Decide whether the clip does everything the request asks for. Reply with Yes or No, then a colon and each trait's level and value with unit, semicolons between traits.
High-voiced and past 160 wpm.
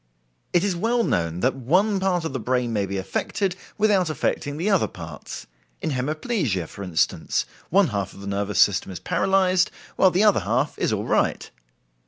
No: medium, 145 Hz; average, 185 wpm